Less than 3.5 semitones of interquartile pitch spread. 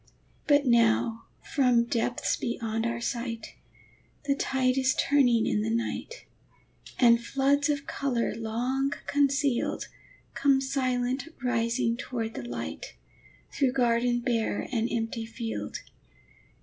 Yes: narrow, 2.6 semitones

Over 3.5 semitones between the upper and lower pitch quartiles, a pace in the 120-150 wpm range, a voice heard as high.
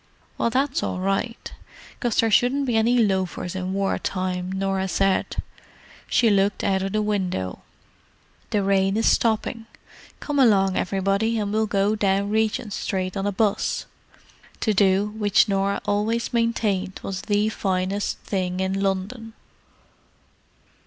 No: narrow, 2.4 semitones; average, 140 wpm; high, 200 Hz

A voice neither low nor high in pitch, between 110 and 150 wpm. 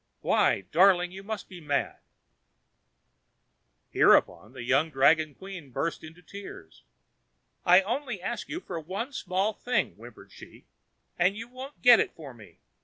Yes: medium, 180 Hz; average, 145 wpm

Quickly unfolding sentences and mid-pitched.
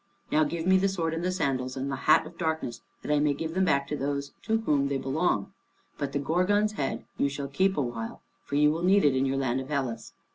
Yes: fast, 255 wpm; medium, 145 Hz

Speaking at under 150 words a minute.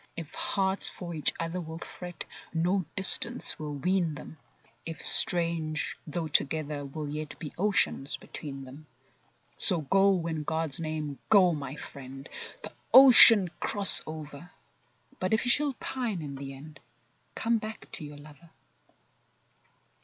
Yes: average, 140 wpm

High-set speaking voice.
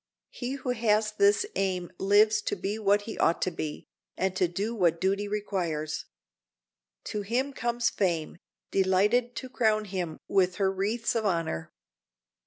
Yes: high, 200 Hz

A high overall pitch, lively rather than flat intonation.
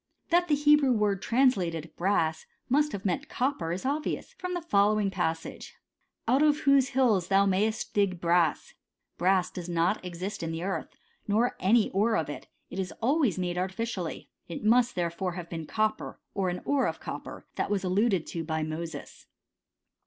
Yes: high, 195 Hz; wide, 5.7 semitones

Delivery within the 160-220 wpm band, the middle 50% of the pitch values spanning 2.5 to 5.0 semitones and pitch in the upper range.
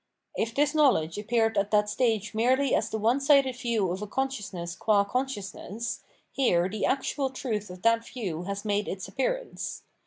Yes: average, 175 wpm; average, 4.5 semitones; high, 225 Hz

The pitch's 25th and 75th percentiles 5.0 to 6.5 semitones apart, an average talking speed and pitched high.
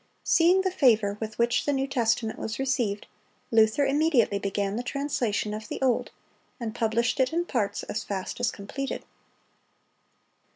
No: average, 4.0 semitones; average, 155 wpm; high, 235 Hz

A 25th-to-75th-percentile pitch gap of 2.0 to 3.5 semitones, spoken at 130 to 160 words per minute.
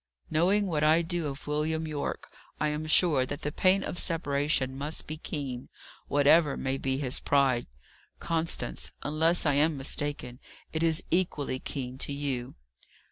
Yes: average, 2.8 semitones; average, 155 wpm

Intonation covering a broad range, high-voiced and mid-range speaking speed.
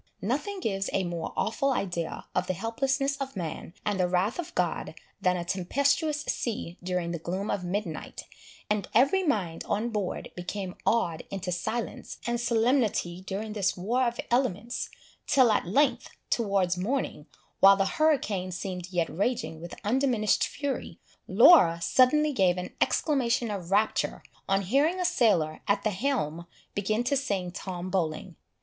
Yes: wide, 5.8 semitones; high, 205 Hz; average, 155 wpm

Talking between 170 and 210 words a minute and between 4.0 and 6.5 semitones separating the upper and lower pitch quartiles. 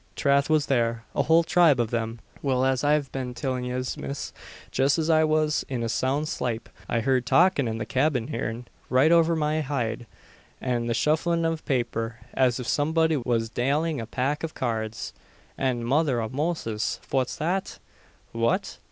Yes: average, 175 wpm; average, 4.5 semitones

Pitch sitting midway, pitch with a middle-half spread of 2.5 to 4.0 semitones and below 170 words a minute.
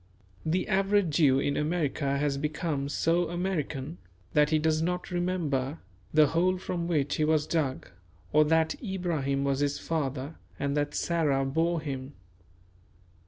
Yes: medium, 155 Hz; average, 3.4 semitones; average, 145 wpm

